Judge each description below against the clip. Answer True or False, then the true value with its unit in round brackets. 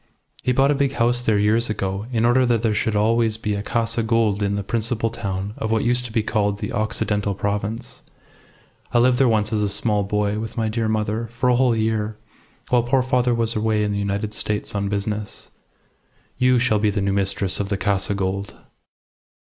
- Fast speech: True (210 wpm)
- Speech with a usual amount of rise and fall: False (2.3 semitones)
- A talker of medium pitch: False (110 Hz)